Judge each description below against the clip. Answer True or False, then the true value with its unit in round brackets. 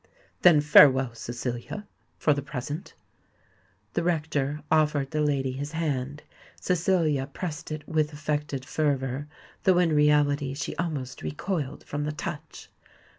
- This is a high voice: False (150 Hz)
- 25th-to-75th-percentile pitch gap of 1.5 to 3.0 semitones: True (2.4 semitones)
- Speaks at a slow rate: True (125 wpm)